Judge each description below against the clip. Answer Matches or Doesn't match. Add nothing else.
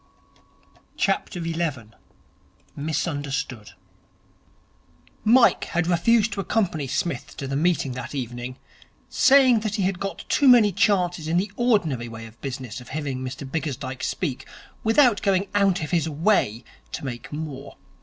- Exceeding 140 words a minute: Doesn't match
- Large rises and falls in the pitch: Matches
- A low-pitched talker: Doesn't match